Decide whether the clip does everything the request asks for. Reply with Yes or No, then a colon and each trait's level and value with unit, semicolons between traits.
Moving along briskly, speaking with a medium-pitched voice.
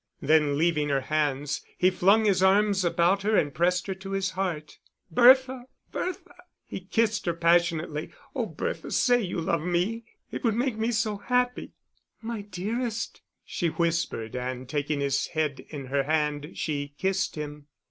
No: average, 160 wpm; medium, 175 Hz